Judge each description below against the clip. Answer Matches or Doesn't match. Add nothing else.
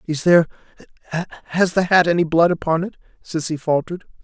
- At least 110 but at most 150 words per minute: Matches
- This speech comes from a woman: Doesn't match